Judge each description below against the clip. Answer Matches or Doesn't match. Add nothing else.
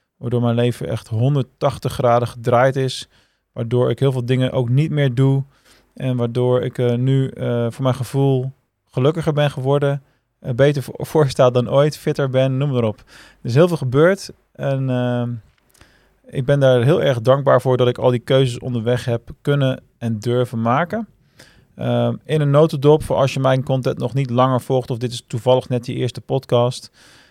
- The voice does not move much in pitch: Matches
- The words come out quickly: Doesn't match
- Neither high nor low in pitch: Doesn't match